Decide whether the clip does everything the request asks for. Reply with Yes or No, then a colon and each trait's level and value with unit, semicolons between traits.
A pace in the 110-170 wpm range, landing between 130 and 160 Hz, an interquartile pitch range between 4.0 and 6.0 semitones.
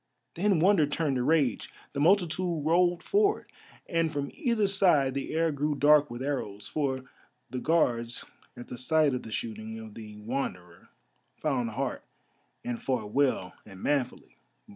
Yes: average, 155 wpm; medium, 140 Hz; average, 5.3 semitones